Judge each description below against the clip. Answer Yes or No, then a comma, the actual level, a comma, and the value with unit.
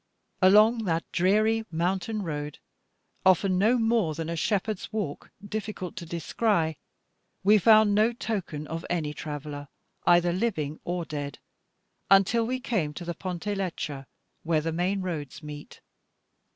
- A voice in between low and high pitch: Yes, medium, 180 Hz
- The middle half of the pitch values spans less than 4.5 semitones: No, average, 4.9 semitones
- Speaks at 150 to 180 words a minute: No, average, 140 wpm